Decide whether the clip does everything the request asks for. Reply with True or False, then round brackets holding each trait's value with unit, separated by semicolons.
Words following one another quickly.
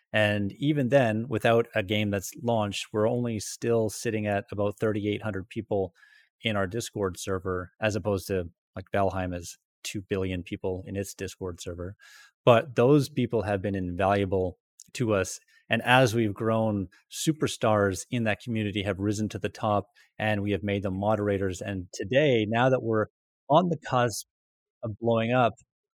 False (165 wpm)